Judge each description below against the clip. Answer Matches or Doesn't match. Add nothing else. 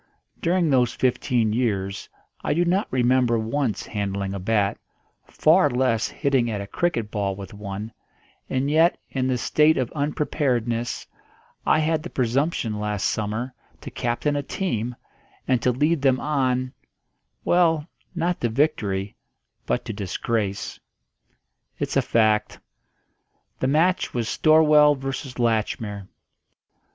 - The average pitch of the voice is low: Matches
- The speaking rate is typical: Doesn't match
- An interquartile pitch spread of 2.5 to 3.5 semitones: Doesn't match